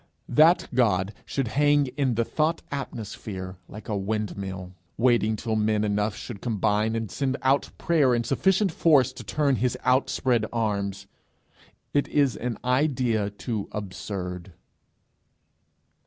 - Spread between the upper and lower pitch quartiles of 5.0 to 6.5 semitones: No, average, 4.5 semitones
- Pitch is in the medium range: No, low, 115 Hz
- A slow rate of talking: Yes, slow, 125 wpm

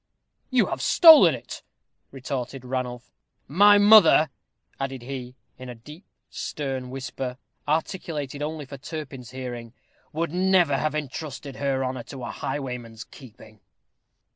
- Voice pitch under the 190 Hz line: Yes, low, 135 Hz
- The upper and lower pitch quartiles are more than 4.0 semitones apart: No, average, 3.5 semitones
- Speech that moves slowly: Yes, slow, 125 wpm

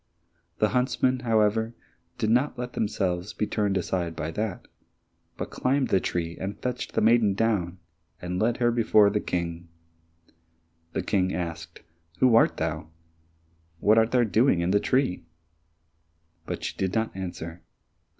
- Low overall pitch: Yes, low, 105 Hz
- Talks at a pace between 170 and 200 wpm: No, average, 150 wpm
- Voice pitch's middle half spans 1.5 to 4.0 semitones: No, average, 4.5 semitones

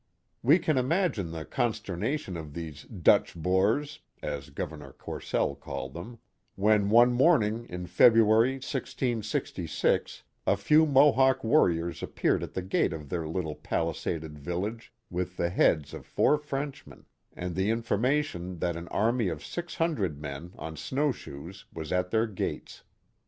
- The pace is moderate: Yes, average, 150 wpm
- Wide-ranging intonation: Yes, wide, 7.3 semitones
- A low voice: Yes, low, 100 Hz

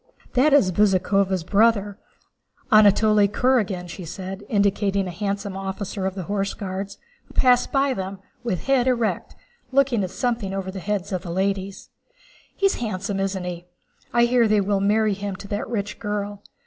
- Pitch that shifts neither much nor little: No, narrow, 2.3 semitones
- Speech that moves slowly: No, average, 165 wpm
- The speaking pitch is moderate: No, high, 200 Hz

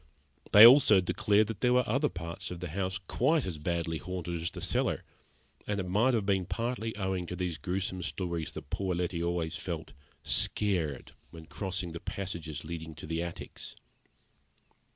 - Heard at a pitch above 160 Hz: No, very low, 90 Hz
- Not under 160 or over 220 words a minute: Yes, average, 175 wpm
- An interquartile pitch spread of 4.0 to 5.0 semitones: No, average, 3.5 semitones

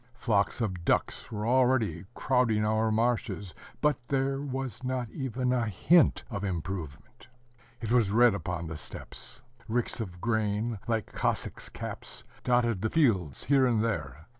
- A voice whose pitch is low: Yes, low, 110 Hz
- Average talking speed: Yes, average, 145 wpm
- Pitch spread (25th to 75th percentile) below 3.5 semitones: No, average, 4.2 semitones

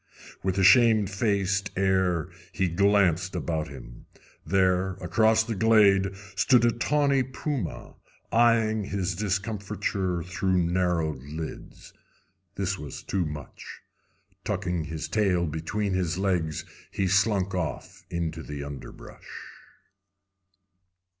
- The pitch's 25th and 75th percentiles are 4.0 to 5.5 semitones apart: No, average, 3.3 semitones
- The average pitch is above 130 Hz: No, very low, 95 Hz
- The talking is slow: Yes, slow, 110 wpm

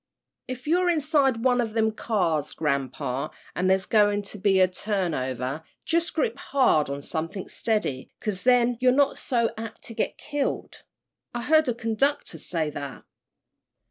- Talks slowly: No, average, 155 wpm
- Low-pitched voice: No, high, 220 Hz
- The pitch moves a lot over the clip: Yes, wide, 7.6 semitones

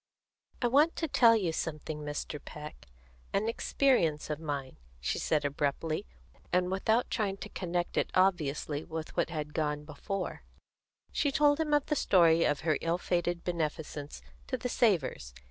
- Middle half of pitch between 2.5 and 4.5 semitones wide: No, wide, 5.6 semitones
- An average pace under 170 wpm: Yes, average, 155 wpm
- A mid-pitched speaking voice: Yes, medium, 170 Hz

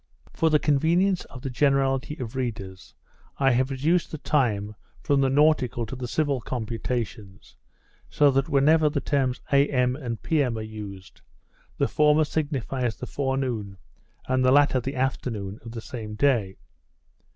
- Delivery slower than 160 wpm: Yes, average, 150 wpm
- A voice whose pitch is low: Yes, low, 130 Hz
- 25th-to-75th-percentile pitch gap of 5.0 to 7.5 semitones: No, average, 3.8 semitones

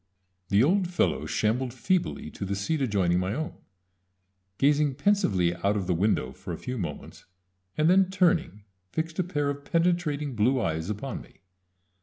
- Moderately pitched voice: No, low, 130 Hz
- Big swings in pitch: Yes, wide, 8.4 semitones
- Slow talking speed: No, average, 170 wpm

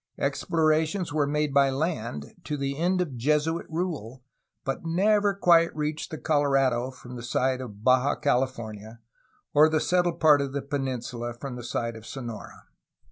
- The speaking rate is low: No, average, 160 wpm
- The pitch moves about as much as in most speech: Yes, average, 4.2 semitones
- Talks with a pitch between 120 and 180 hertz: Yes, medium, 140 Hz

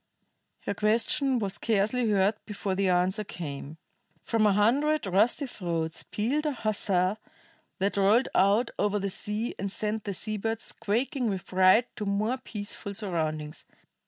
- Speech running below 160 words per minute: Yes, average, 150 wpm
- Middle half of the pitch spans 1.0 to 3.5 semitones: Yes, average, 3.0 semitones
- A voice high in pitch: Yes, high, 210 Hz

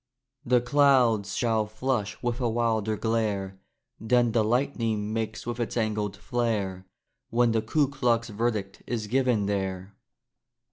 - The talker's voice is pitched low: Yes, low, 115 Hz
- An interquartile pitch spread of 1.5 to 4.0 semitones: Yes, narrow, 2.6 semitones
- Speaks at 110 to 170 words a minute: Yes, slow, 135 wpm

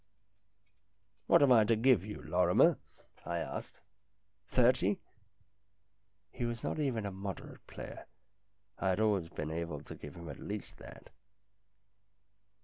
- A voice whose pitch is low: Yes, low, 100 Hz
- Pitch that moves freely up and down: No, average, 3.1 semitones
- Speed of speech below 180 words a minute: Yes, average, 150 wpm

